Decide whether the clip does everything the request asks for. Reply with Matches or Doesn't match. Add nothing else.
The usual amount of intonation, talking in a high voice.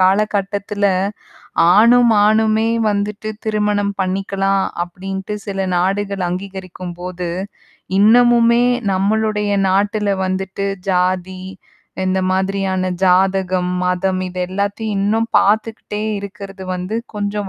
Doesn't match